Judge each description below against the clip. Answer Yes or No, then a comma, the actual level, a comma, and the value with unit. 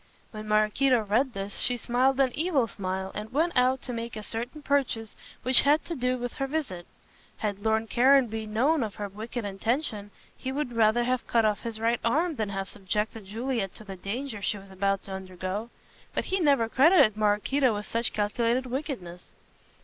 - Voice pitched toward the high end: Yes, high, 230 Hz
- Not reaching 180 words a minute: No, average, 190 wpm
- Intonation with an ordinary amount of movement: Yes, average, 4.1 semitones